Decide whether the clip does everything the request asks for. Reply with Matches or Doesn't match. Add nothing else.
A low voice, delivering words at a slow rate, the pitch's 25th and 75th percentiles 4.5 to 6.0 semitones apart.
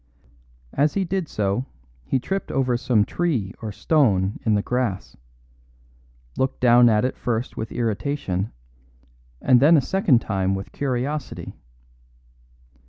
Matches